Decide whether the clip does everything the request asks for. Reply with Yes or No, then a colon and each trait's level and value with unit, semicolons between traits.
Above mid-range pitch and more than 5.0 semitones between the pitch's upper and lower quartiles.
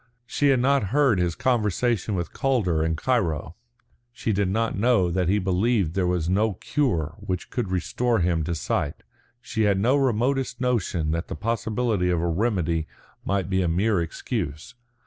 No: low, 100 Hz; wide, 5.6 semitones